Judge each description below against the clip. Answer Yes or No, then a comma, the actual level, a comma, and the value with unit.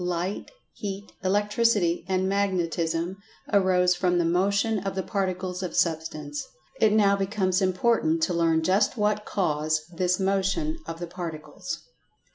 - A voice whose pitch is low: No, medium, 185 Hz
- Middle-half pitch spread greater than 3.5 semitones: No, average, 2.8 semitones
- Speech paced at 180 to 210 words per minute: No, slow, 135 wpm